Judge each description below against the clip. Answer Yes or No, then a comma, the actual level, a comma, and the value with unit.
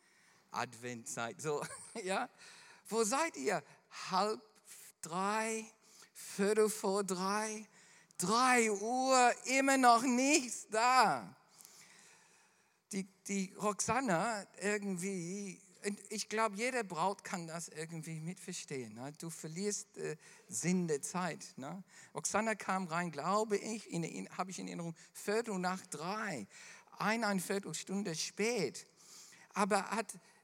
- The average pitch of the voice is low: No, high, 200 Hz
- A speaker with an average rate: No, slow, 105 wpm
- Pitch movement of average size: Yes, average, 3.7 semitones